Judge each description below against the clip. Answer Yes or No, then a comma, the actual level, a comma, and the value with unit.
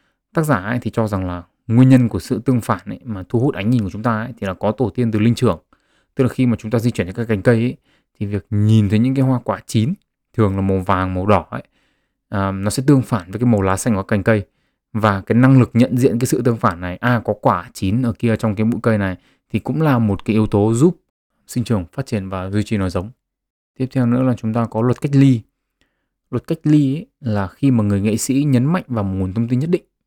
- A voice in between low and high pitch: No, low, 115 Hz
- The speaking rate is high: Yes, fast, 285 wpm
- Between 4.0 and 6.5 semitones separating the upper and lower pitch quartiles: No, average, 3.3 semitones